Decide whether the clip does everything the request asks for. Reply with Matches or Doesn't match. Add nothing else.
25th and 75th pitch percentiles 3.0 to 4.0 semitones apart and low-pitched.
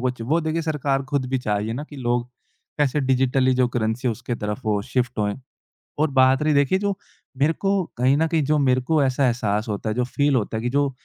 Matches